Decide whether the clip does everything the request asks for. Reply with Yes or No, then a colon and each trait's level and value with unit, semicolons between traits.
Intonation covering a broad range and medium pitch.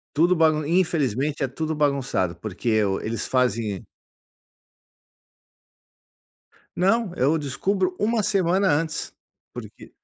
Yes: wide, 6.5 semitones; medium, 150 Hz